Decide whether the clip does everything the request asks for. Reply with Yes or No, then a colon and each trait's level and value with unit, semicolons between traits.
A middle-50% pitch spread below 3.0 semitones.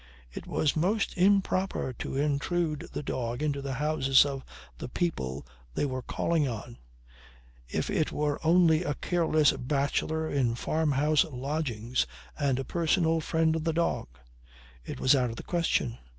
No: average, 3.5 semitones